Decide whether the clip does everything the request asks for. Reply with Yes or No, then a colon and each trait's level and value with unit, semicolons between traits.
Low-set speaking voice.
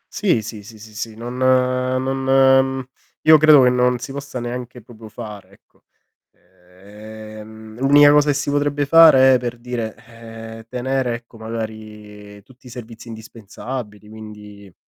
Yes: low, 120 Hz